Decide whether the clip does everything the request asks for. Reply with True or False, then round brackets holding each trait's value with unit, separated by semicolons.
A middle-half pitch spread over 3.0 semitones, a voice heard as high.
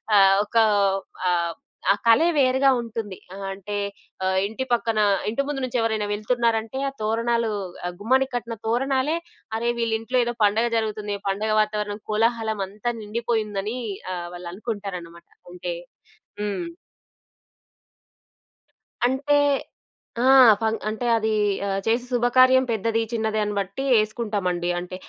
False (2.7 semitones; 220 Hz)